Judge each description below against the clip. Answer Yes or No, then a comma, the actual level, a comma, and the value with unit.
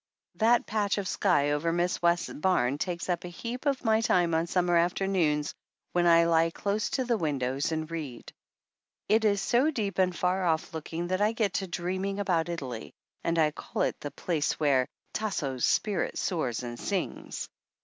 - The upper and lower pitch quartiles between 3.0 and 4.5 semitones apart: Yes, average, 4.0 semitones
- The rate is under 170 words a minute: No, average, 185 wpm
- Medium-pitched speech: Yes, medium, 175 Hz